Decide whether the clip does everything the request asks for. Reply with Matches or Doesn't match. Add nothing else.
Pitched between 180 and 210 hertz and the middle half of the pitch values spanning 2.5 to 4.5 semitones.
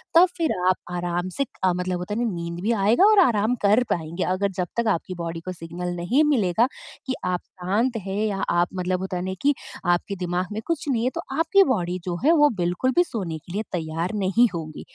Doesn't match